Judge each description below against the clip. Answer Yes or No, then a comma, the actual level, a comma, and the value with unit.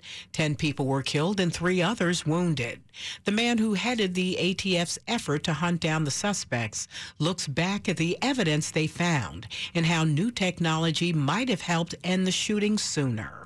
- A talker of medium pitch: Yes, medium, 170 Hz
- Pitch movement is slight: No, average, 3.7 semitones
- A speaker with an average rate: Yes, average, 170 wpm